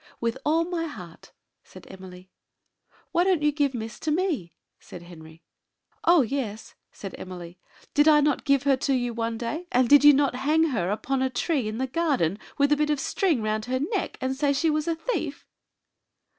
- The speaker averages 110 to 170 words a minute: No, average, 200 wpm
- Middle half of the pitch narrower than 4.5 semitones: No, wide, 5.6 semitones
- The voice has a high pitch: Yes, very high, 270 Hz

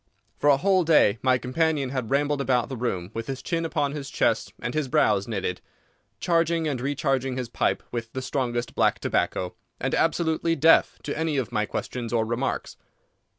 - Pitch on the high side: No, low, 135 Hz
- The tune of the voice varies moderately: Yes, average, 4.4 semitones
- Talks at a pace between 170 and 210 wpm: Yes, average, 185 wpm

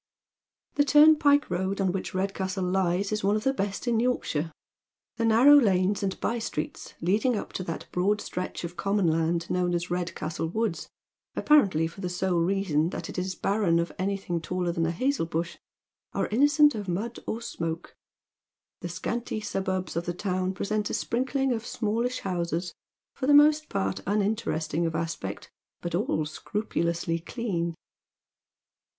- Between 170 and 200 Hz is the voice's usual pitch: Yes, high, 190 Hz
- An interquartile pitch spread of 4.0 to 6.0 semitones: Yes, average, 4.5 semitones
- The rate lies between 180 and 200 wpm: No, average, 165 wpm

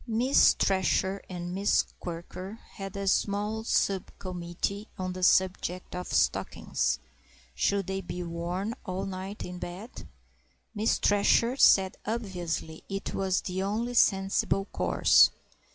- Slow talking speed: Yes, slow, 120 wpm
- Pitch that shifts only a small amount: Yes, narrow, 2.1 semitones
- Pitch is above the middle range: Yes, high, 195 Hz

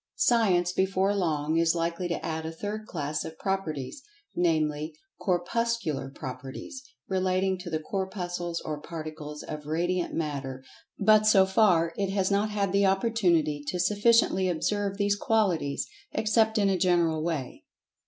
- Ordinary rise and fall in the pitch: Yes, average, 4.0 semitones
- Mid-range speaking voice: Yes, medium, 180 Hz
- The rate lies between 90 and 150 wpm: Yes, average, 145 wpm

